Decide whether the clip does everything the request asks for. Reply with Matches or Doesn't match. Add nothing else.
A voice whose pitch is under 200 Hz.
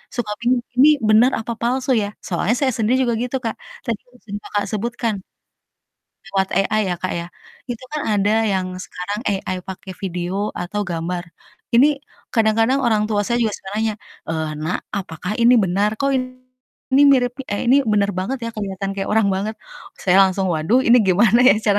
Doesn't match